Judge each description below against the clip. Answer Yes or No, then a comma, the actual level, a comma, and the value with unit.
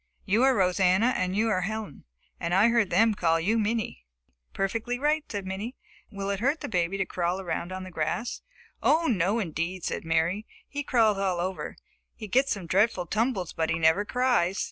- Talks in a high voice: Yes, high, 195 Hz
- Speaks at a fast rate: No, average, 190 wpm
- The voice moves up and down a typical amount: Yes, average, 4.2 semitones